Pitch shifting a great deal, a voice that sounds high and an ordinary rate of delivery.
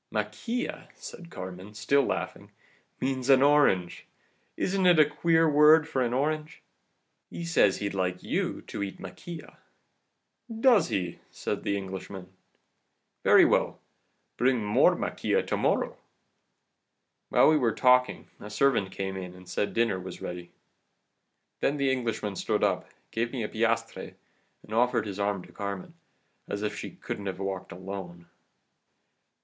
No: wide, 6.7 semitones; low, 110 Hz; average, 145 wpm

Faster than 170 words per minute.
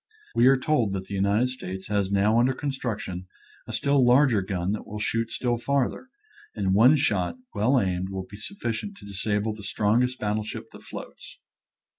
Yes: average, 180 wpm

